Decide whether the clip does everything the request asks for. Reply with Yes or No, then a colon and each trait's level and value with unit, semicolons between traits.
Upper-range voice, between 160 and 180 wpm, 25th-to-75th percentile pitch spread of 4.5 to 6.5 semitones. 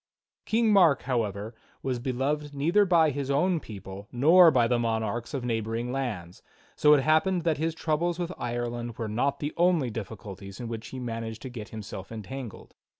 No: low, 125 Hz; average, 175 wpm; wide, 5.5 semitones